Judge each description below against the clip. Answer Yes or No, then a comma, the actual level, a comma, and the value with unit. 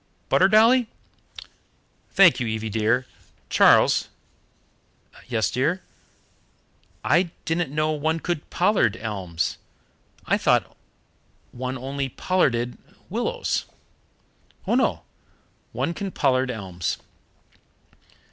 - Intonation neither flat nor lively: No, wide, 7.3 semitones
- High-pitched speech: No, low, 130 Hz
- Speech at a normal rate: No, slow, 95 wpm